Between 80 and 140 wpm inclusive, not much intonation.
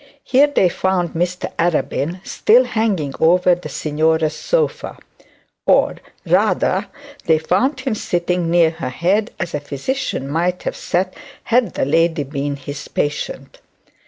No: slow, 135 wpm; average, 3.6 semitones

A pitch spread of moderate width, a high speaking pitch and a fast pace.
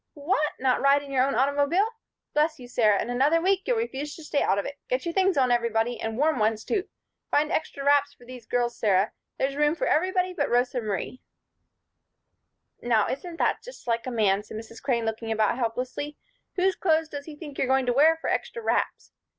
Yes: average, 4.7 semitones; very high, 270 Hz; fast, 210 wpm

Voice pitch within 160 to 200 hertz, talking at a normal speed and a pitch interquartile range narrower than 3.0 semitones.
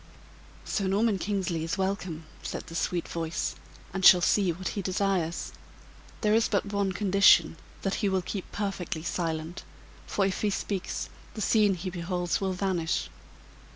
Yes: high, 190 Hz; average, 155 wpm; narrow, 2.5 semitones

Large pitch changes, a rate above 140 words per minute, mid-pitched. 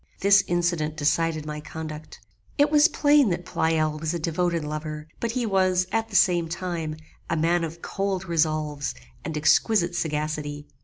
No: average, 3.3 semitones; average, 160 wpm; medium, 165 Hz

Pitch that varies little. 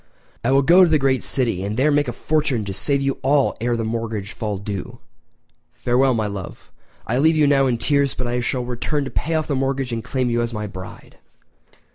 No: average, 3.5 semitones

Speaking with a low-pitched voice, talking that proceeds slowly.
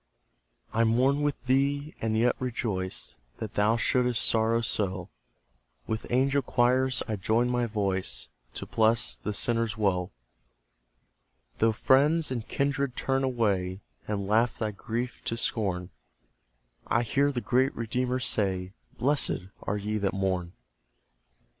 Yes: low, 115 Hz; slow, 130 wpm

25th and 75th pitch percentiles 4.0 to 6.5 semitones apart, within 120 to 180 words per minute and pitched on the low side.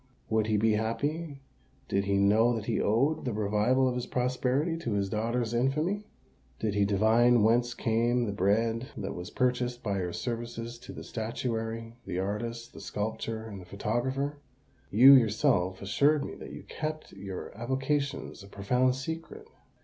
No: average, 3.6 semitones; average, 165 wpm; low, 115 Hz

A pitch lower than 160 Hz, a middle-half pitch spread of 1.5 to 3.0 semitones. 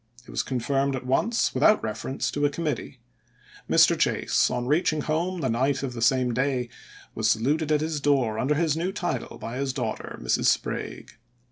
No: medium, 140 Hz; average, 3.5 semitones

